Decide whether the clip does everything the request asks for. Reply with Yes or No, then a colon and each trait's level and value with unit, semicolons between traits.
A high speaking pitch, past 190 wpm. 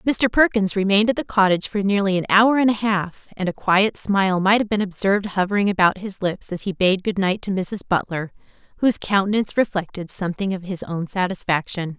Yes: high, 195 Hz; fast, 205 wpm